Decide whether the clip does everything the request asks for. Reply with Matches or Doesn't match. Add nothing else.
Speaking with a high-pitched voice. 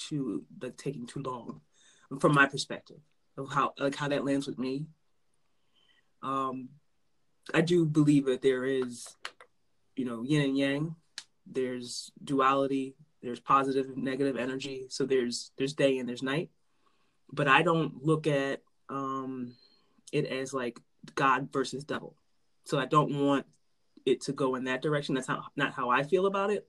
Doesn't match